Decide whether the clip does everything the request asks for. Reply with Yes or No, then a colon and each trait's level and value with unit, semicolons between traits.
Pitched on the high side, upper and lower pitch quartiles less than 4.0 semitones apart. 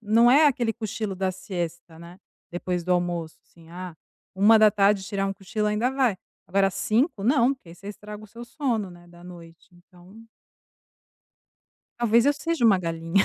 No: high, 195 Hz; average, 4.3 semitones